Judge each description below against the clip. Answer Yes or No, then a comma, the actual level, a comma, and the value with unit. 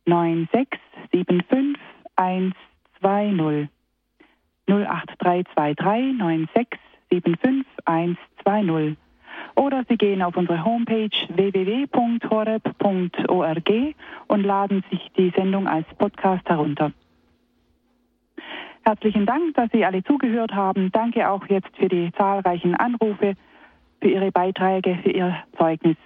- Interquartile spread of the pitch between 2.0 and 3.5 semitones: No, average, 4.1 semitones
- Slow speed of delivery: Yes, slow, 90 wpm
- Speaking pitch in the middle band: No, high, 195 Hz